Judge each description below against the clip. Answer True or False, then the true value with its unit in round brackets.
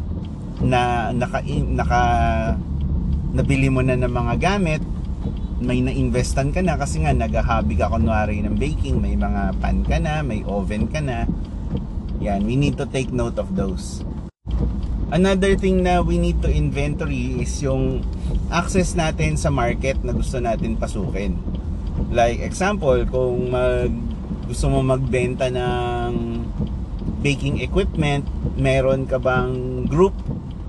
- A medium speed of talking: True (135 wpm)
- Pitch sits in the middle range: False (100 Hz)